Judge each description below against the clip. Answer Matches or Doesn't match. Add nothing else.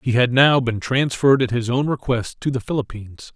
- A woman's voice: Doesn't match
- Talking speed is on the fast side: Matches